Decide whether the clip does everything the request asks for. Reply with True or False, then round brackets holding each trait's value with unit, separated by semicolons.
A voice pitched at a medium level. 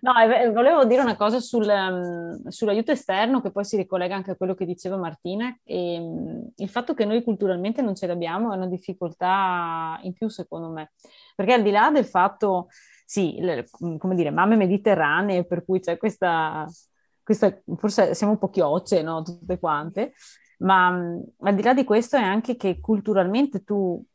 False (195 Hz)